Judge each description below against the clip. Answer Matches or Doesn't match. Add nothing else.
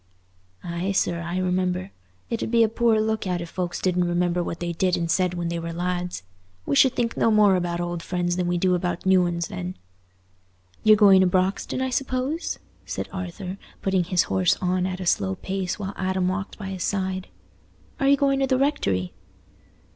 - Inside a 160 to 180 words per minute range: Doesn't match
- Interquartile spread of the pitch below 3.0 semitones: Matches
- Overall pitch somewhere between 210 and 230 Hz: Doesn't match